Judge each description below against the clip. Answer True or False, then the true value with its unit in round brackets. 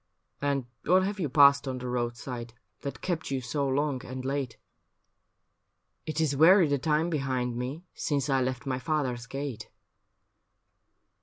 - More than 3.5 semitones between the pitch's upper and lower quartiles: False (3.0 semitones)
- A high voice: False (140 Hz)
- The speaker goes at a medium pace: True (165 wpm)